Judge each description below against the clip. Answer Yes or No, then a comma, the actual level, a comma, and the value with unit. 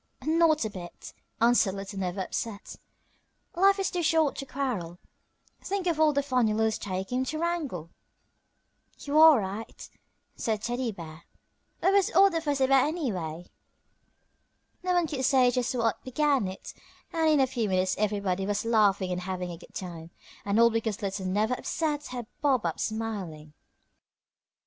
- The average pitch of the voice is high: Yes, high, 230 Hz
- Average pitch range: No, wide, 7.4 semitones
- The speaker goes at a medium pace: Yes, average, 165 wpm